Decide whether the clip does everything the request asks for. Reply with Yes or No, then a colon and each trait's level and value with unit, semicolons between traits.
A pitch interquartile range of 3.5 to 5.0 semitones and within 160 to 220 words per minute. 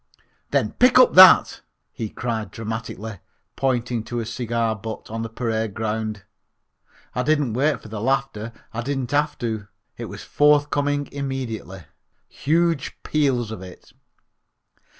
No: average, 4.3 semitones; slow, 135 wpm